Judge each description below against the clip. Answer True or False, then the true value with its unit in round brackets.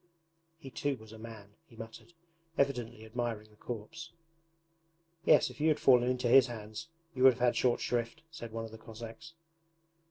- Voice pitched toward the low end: True (120 Hz)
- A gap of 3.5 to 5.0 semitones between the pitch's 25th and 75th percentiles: False (2.9 semitones)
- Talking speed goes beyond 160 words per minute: True (180 wpm)